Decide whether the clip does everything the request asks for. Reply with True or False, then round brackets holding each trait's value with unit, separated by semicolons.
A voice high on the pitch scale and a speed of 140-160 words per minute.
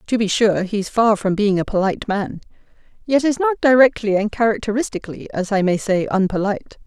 False (215 Hz; 190 wpm)